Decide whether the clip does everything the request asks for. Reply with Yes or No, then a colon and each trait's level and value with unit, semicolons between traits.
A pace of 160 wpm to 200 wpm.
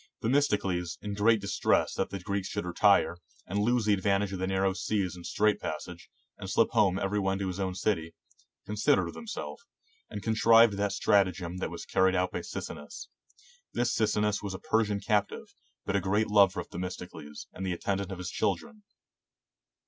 Yes: average, 180 wpm